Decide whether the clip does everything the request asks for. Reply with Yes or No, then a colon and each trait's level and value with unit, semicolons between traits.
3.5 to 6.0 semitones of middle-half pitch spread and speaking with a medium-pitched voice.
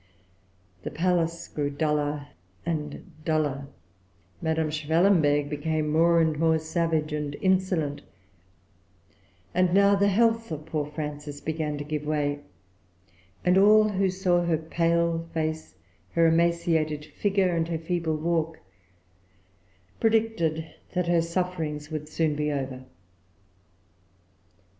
No: narrow, 2.5 semitones; medium, 160 Hz